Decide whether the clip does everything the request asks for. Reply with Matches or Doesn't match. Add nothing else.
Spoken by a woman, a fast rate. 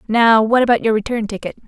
Matches